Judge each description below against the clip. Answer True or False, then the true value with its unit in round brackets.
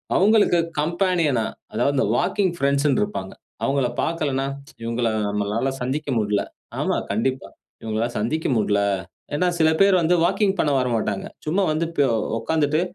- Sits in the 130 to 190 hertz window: True (140 Hz)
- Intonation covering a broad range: True (6.4 semitones)